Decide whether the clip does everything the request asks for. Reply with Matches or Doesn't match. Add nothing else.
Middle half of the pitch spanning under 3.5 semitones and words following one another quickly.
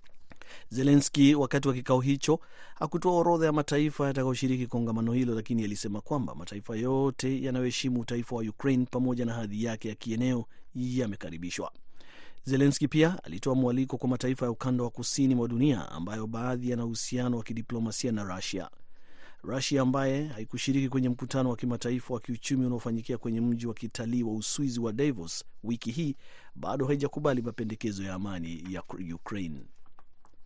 Matches